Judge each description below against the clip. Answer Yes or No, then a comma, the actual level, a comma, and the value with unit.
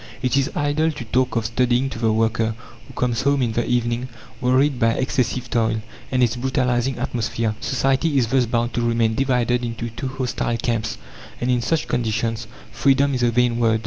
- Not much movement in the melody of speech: Yes, narrow, 2.1 semitones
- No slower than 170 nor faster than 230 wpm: Yes, average, 190 wpm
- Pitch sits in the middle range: No, low, 120 Hz